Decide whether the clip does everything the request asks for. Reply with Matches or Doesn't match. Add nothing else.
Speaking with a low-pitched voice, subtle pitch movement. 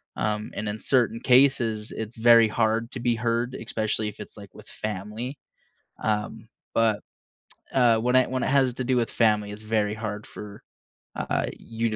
Matches